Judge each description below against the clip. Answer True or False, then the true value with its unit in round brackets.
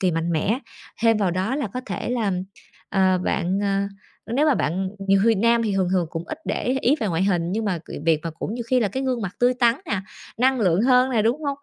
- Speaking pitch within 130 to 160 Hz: False (210 Hz)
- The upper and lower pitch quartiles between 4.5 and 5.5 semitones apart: True (5.1 semitones)